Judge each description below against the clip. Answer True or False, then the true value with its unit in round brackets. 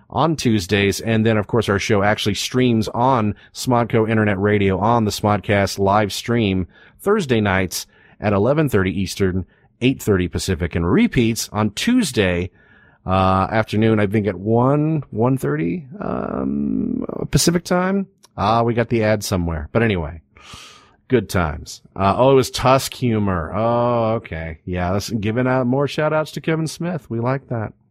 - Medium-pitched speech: False (110 Hz)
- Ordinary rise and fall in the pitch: True (4.8 semitones)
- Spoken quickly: False (150 wpm)